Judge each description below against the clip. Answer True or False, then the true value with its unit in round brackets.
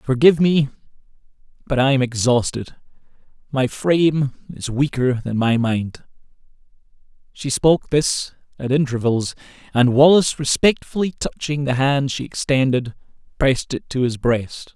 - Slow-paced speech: True (120 wpm)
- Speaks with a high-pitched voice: False (135 Hz)